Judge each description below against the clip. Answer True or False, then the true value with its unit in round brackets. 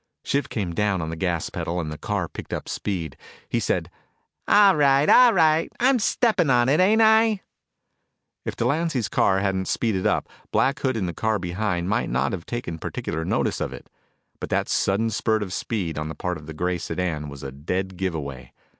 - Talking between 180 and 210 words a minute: True (200 wpm)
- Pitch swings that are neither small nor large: False (8.5 semitones)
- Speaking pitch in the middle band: False (95 Hz)